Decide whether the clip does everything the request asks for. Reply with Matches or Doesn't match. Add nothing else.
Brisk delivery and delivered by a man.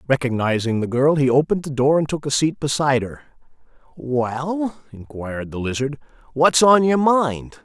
Doesn't match